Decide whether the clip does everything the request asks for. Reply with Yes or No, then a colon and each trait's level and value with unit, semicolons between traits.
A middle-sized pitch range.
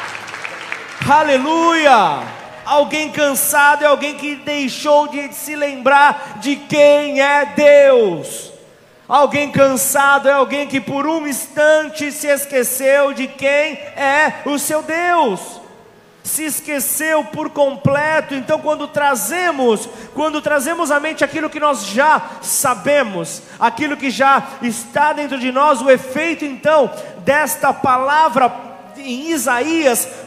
No: narrow, 1.8 semitones